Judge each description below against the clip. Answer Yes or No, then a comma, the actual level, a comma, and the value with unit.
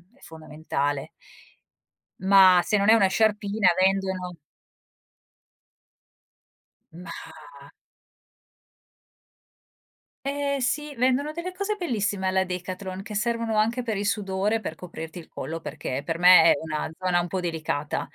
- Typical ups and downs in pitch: Yes, average, 4.4 semitones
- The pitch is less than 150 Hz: No, high, 190 Hz